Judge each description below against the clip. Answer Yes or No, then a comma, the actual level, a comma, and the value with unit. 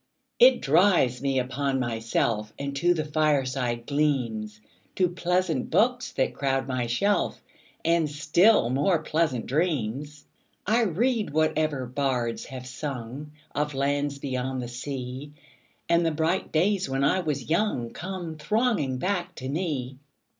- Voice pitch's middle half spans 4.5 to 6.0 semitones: Yes, average, 4.8 semitones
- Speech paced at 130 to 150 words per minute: Yes, average, 145 wpm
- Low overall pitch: No, medium, 145 Hz